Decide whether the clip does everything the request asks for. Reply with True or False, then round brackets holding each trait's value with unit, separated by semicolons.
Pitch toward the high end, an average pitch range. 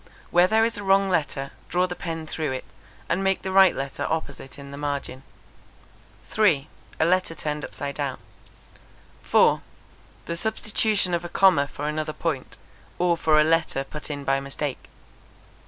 False (160 Hz; 4.5 semitones)